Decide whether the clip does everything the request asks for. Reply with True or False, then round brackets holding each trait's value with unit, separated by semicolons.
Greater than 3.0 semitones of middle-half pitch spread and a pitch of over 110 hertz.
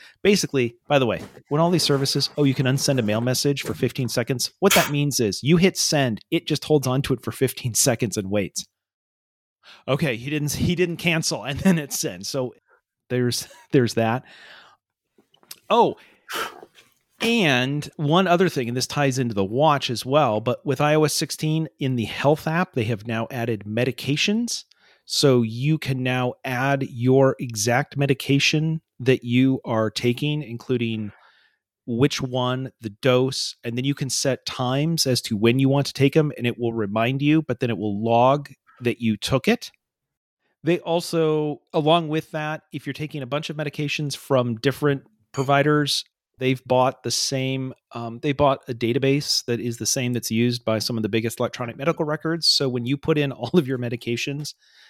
True (3.6 semitones; 135 Hz)